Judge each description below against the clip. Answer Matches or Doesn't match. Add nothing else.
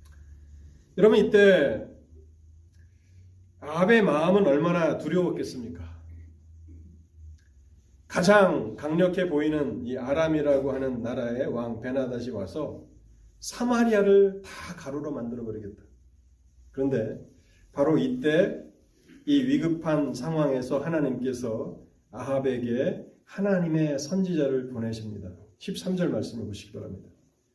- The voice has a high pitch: Doesn't match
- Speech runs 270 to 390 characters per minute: Doesn't match